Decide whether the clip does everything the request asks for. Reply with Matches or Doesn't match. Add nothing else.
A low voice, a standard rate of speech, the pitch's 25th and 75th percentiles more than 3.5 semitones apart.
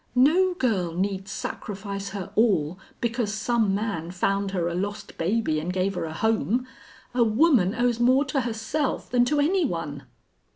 Doesn't match